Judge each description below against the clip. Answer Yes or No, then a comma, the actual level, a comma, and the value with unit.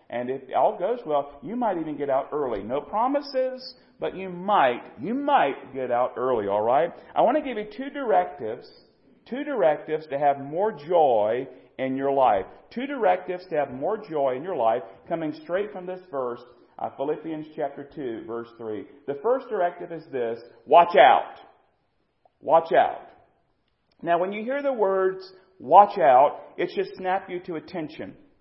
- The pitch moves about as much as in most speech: No, wide, 7.9 semitones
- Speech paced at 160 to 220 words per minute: Yes, average, 170 wpm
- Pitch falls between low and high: Yes, medium, 175 Hz